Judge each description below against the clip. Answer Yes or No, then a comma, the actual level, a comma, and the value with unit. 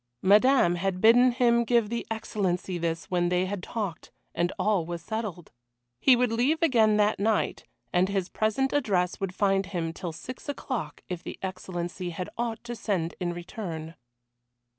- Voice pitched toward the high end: Yes, high, 195 Hz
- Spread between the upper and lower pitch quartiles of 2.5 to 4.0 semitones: No, average, 4.5 semitones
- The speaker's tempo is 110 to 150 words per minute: No, average, 165 wpm